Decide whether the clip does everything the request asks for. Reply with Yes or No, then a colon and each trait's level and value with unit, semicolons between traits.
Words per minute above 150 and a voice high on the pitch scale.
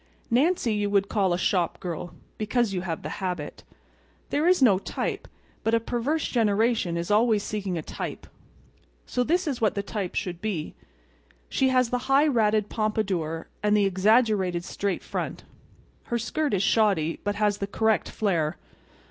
Yes: average, 165 wpm; high, 210 Hz